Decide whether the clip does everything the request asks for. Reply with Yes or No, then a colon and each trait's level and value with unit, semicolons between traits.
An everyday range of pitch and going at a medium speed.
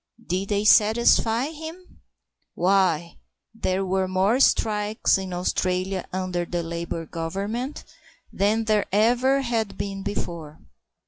No: average, 3.5 semitones; slow, 115 wpm